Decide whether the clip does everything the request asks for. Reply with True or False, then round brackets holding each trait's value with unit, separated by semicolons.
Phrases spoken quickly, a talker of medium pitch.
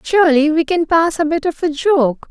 False (235 wpm; 315 Hz)